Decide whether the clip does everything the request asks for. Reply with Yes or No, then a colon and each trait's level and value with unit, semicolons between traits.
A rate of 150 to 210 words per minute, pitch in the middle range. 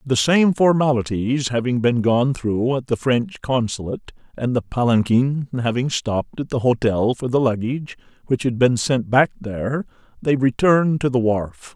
No: average, 170 wpm; low, 125 Hz